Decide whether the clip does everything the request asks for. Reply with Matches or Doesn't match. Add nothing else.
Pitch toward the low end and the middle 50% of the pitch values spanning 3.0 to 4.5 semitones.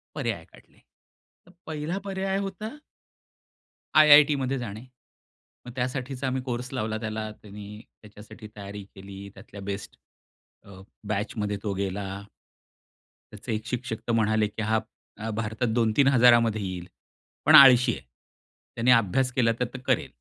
Matches